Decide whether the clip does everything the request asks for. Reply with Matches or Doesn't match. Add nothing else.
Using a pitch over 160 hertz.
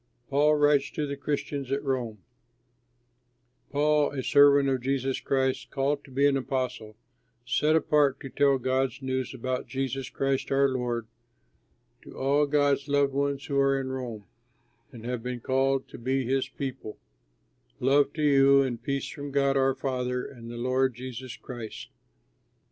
Doesn't match